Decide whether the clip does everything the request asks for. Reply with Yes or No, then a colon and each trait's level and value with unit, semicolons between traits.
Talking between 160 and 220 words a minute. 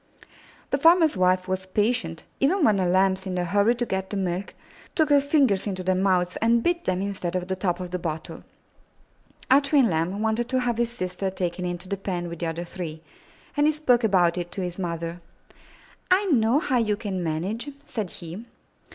Yes: fast, 205 wpm